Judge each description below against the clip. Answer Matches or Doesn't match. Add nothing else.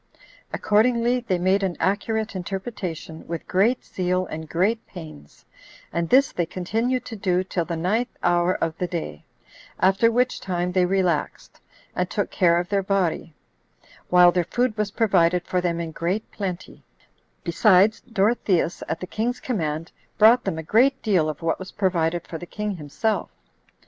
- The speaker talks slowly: Doesn't match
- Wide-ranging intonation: Doesn't match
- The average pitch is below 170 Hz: Doesn't match